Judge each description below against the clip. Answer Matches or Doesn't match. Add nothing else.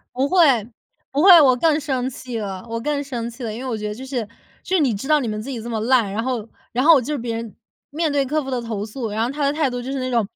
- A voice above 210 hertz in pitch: Matches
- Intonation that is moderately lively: Matches